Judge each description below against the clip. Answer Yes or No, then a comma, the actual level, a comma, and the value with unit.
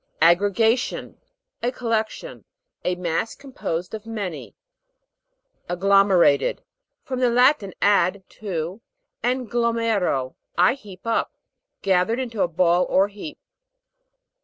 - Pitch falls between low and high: No, high, 205 Hz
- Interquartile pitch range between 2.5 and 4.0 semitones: No, average, 4.4 semitones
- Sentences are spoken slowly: Yes, slow, 105 wpm